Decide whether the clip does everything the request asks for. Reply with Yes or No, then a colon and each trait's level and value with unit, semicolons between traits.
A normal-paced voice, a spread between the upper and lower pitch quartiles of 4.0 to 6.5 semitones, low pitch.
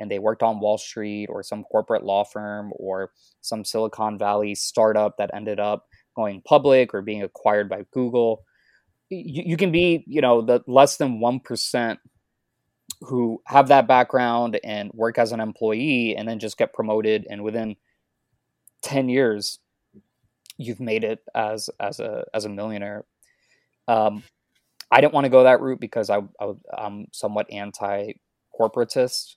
No: average, 155 wpm; average, 2.9 semitones; low, 110 Hz